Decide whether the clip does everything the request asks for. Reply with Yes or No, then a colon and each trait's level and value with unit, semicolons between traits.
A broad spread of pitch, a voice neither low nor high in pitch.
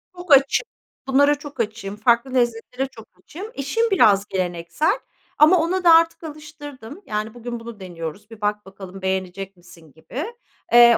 No: wide, 7.0 semitones; high, 235 Hz